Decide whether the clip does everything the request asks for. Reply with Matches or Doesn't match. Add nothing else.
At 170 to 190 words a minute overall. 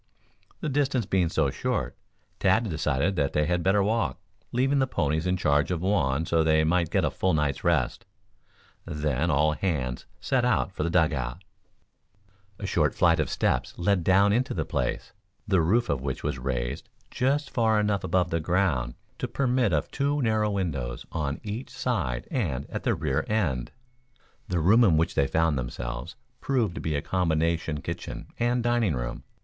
Matches